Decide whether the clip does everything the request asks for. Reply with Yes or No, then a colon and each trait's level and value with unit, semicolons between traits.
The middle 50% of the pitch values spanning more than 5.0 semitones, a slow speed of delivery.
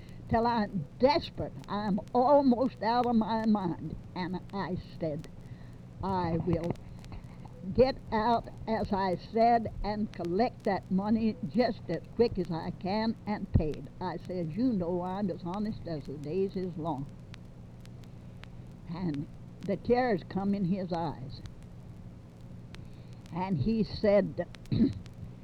Yes: wide, 5.6 semitones; slow, 125 wpm